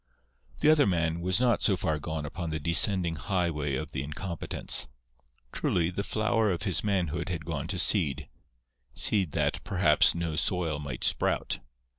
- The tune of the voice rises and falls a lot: No, average, 4.0 semitones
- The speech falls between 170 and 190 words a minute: No, average, 155 wpm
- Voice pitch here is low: Yes, very low, 85 Hz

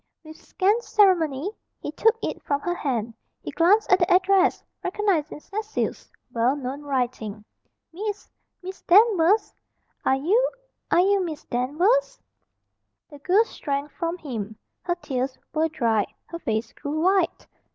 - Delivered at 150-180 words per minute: No, average, 140 wpm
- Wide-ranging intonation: Yes, wide, 6.2 semitones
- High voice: Yes, very high, 330 Hz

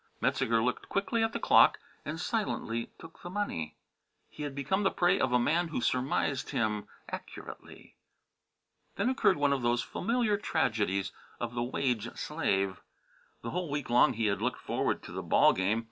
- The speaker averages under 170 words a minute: No, average, 175 wpm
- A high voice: No, low, 130 Hz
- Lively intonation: Yes, wide, 7.5 semitones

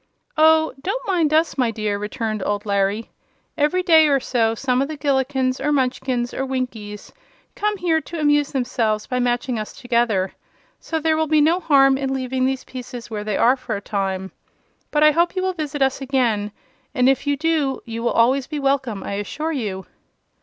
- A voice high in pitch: Yes, very high, 265 Hz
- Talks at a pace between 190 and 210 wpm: Yes, average, 195 wpm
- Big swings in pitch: No, average, 4.7 semitones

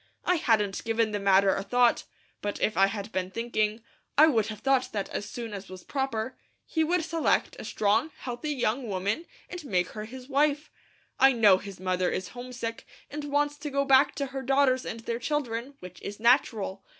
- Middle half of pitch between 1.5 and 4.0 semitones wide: No, average, 5.2 semitones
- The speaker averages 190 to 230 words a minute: Yes, average, 200 wpm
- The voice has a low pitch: No, high, 235 Hz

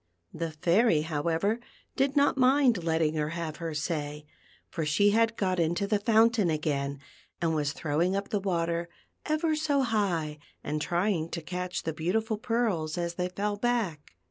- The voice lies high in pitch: No, medium, 175 Hz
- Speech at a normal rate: Yes, average, 165 wpm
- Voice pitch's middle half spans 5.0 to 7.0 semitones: Yes, wide, 5.6 semitones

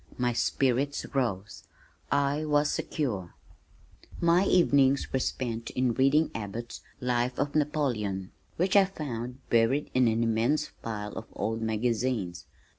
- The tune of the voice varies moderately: Yes, average, 4.1 semitones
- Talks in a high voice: No, low, 125 Hz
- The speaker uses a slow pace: Yes, slow, 125 wpm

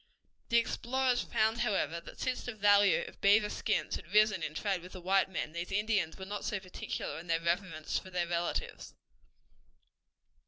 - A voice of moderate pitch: No, high, 195 Hz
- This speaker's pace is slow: No, average, 180 wpm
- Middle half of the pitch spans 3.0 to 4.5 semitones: Yes, average, 3.7 semitones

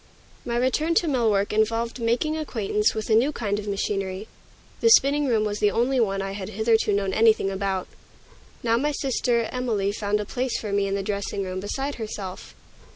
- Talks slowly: No, average, 195 wpm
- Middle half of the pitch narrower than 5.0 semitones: Yes, average, 3.6 semitones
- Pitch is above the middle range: Yes, high, 215 Hz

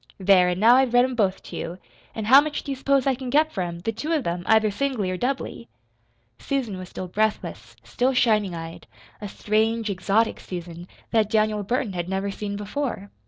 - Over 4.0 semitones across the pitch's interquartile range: Yes, average, 5.2 semitones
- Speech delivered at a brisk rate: Yes, fast, 210 wpm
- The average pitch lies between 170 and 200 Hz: No, high, 215 Hz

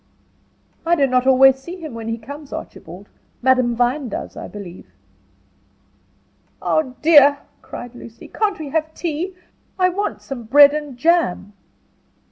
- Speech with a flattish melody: No, average, 4.7 semitones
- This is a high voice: Yes, very high, 270 Hz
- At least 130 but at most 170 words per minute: Yes, average, 140 wpm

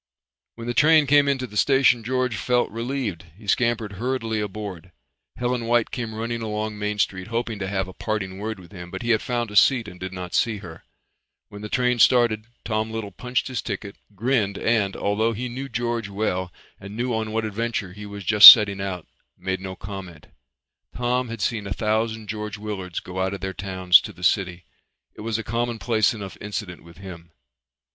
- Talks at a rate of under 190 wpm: No, average, 200 wpm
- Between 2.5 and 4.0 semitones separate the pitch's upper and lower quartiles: Yes, average, 3.4 semitones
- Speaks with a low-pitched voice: Yes, low, 110 Hz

